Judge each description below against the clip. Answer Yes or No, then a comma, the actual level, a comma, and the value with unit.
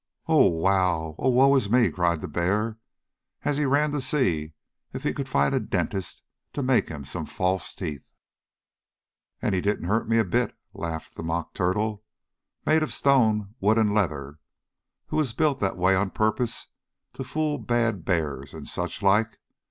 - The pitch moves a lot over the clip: Yes, wide, 6.0 semitones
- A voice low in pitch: Yes, low, 100 Hz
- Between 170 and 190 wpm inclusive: Yes, average, 175 wpm